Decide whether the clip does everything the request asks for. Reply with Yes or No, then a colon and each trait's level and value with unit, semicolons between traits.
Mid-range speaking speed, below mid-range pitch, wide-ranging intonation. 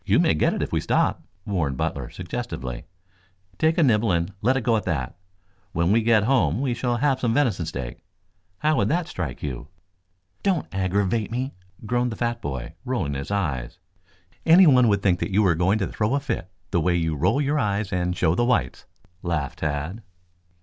Yes: average, 190 wpm; low, 100 Hz; wide, 6.7 semitones